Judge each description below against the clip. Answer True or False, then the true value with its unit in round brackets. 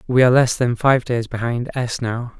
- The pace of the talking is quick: True (225 wpm)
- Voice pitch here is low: True (120 Hz)